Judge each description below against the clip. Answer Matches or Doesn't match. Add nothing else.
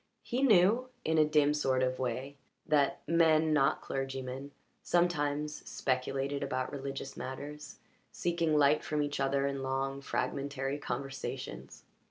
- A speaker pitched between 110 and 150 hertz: Matches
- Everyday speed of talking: Doesn't match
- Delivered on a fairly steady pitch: Matches